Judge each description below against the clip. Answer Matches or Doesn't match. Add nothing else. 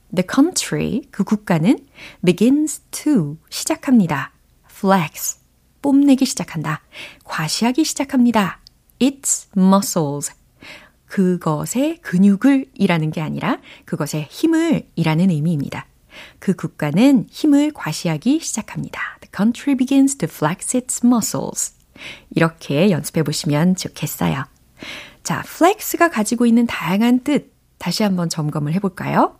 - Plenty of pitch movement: Matches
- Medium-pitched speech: Doesn't match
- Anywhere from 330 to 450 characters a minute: Matches